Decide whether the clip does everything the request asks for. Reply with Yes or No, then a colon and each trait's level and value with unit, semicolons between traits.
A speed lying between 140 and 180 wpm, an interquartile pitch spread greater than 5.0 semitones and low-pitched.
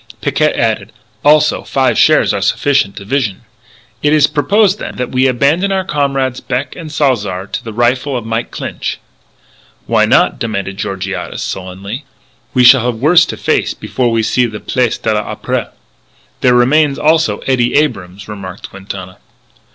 Yes: average, 155 wpm; wide, 5.5 semitones; low, 125 Hz